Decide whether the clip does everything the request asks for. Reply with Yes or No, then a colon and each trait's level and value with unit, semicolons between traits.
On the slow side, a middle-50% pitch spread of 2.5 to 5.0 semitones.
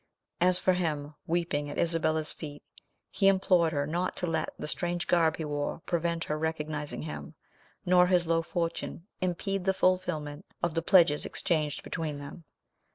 No: average, 160 wpm; average, 2.8 semitones